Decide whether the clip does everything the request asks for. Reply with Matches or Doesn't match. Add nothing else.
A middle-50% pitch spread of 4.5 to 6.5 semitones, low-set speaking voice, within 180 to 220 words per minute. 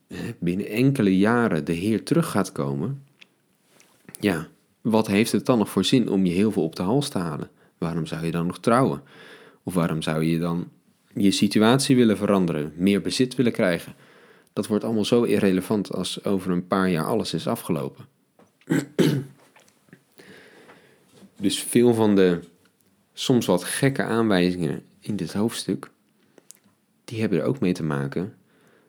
Doesn't match